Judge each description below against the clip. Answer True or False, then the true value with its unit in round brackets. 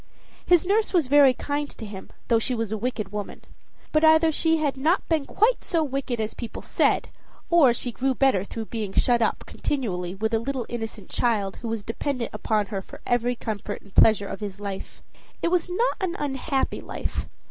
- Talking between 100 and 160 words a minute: False (200 wpm)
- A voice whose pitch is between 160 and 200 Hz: False (245 Hz)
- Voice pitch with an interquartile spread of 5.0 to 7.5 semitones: True (5.4 semitones)